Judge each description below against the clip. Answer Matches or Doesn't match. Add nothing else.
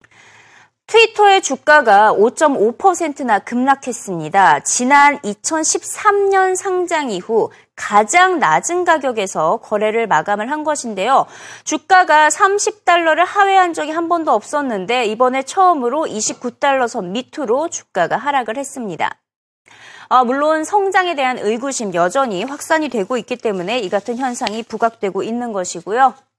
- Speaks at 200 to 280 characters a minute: Matches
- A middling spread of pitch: Doesn't match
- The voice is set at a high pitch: Matches